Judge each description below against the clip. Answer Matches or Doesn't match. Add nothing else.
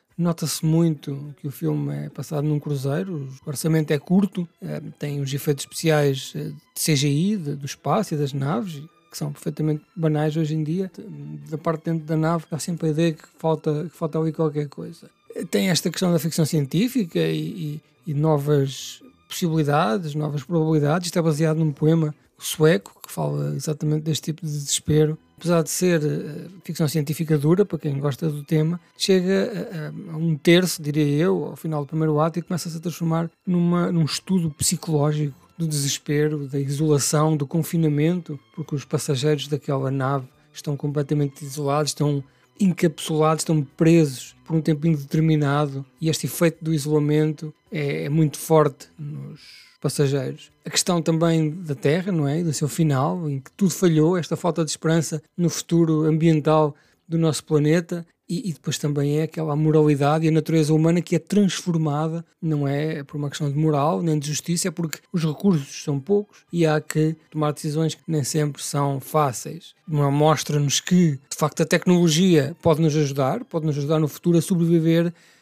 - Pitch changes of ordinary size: Doesn't match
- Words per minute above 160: Matches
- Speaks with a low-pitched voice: Doesn't match